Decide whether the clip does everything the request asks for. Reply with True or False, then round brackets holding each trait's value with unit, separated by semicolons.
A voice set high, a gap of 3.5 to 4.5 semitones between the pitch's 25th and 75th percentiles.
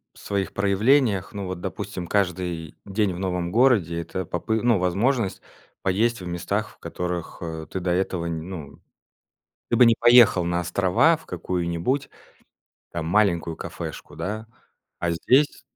False (95 Hz; 4.2 semitones)